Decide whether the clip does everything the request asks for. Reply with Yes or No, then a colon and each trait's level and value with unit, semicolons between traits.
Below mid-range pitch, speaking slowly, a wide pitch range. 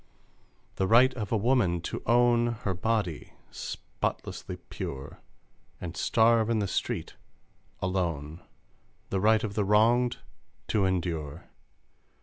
No: low, 105 Hz; slow, 120 wpm; average, 4.8 semitones